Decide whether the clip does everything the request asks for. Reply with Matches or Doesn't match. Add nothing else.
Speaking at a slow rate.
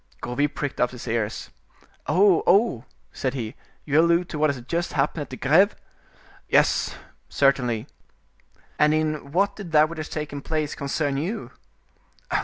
Doesn't match